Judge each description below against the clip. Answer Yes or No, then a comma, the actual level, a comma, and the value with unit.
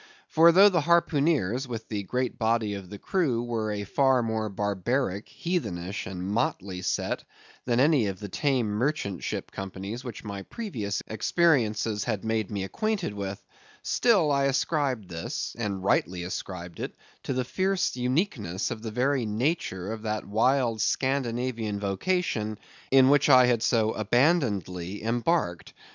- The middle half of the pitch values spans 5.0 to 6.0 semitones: Yes, average, 5.3 semitones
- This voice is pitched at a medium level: No, low, 115 Hz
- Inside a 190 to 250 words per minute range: No, average, 145 wpm